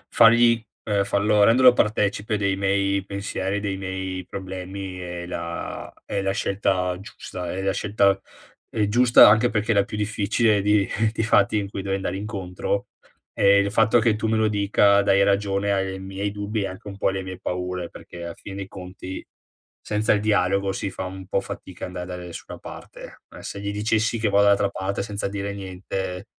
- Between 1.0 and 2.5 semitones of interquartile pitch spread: Yes, narrow, 1.6 semitones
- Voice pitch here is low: Yes, low, 100 Hz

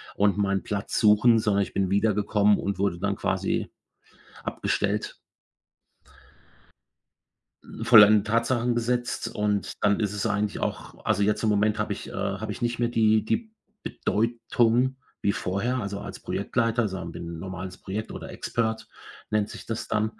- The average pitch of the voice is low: Yes, low, 105 Hz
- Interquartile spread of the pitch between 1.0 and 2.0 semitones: No, narrow, 2.4 semitones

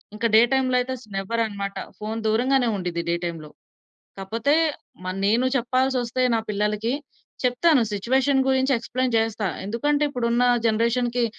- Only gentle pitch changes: No, average, 3.4 semitones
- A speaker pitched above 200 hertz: Yes, high, 235 Hz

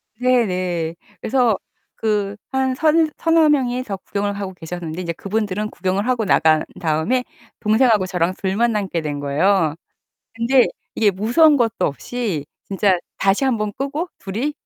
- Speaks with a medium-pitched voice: No, high, 205 Hz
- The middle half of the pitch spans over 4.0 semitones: Yes, average, 5.2 semitones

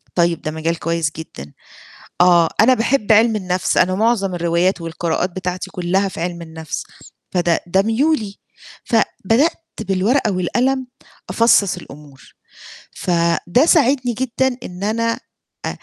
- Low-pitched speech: No, medium, 185 Hz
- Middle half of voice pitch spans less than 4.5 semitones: No, average, 5.2 semitones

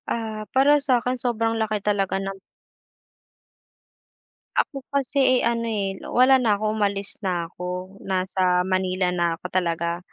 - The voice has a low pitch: No, high, 200 Hz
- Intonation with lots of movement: No, average, 4.3 semitones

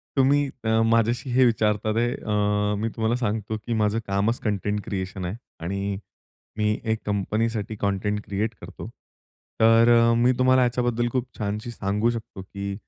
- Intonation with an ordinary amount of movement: No, narrow, 2.3 semitones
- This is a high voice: No, low, 110 Hz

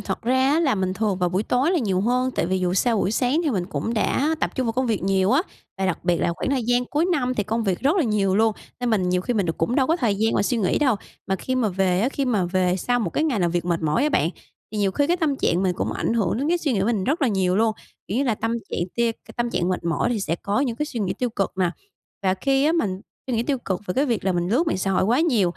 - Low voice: No, high, 220 Hz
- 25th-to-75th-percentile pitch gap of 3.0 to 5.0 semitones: No, wide, 5.6 semitones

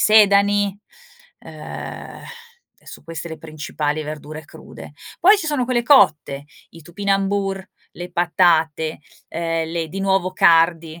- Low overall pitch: No, medium, 170 Hz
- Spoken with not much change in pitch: No, average, 3.9 semitones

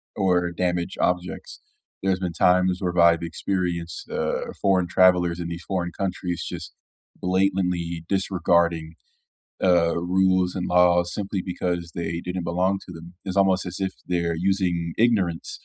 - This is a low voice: Yes, very low, 90 Hz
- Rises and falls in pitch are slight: Yes, narrow, 1.4 semitones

